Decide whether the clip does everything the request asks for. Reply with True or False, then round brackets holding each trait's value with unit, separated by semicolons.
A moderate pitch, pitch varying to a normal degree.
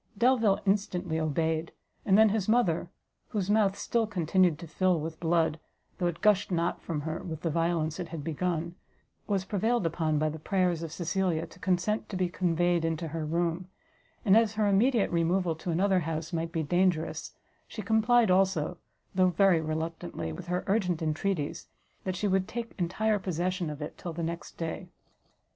True (175 Hz; 3.0 semitones)